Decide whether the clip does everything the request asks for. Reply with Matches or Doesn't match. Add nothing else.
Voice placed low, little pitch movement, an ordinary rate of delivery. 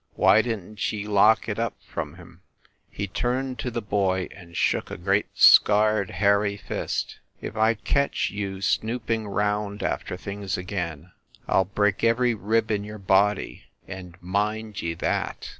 Matches